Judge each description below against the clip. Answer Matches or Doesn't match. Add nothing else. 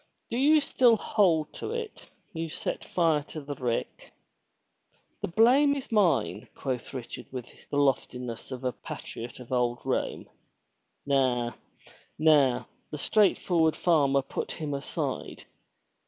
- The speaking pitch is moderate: Matches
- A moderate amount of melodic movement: Doesn't match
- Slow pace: Matches